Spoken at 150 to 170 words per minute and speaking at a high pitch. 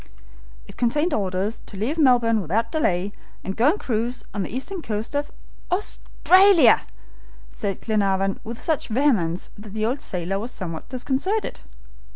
Yes: average, 155 wpm; high, 225 Hz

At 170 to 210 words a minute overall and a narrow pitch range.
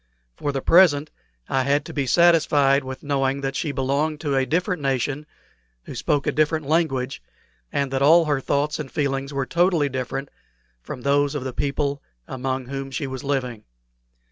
Yes: average, 175 wpm; narrow, 1.9 semitones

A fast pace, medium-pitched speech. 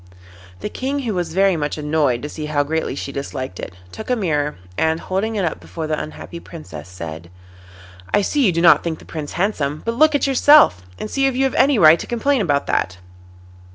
Yes: fast, 220 wpm; medium, 165 Hz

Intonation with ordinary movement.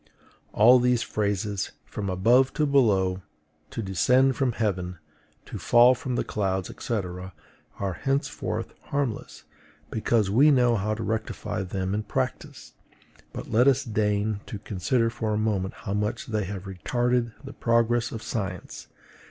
Yes: average, 3.9 semitones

